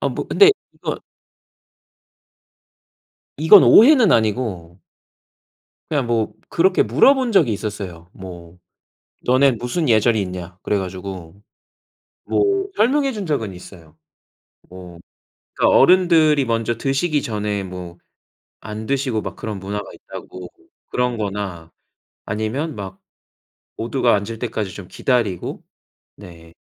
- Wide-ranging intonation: Yes, wide, 6.9 semitones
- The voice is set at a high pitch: No, low, 110 Hz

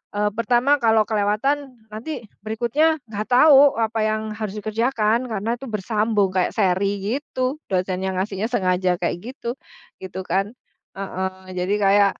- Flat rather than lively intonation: No, average, 3.7 semitones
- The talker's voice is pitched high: Yes, high, 215 Hz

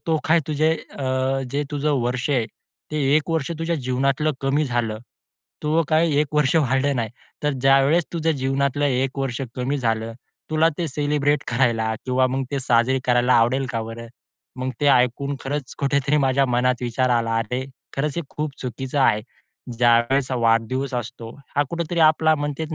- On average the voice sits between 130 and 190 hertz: Yes, low, 135 Hz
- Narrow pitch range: No, average, 3.2 semitones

